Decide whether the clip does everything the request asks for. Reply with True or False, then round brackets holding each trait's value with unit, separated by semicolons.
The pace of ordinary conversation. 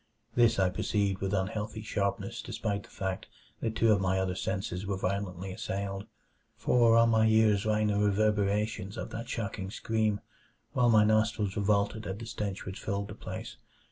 True (175 wpm)